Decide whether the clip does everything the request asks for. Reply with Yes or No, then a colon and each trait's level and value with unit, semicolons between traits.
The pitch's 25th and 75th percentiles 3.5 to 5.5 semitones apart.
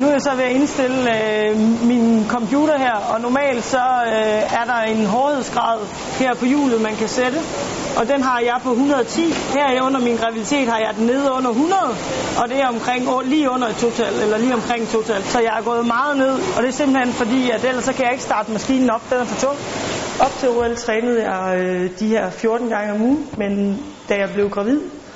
No: average, 2.9 semitones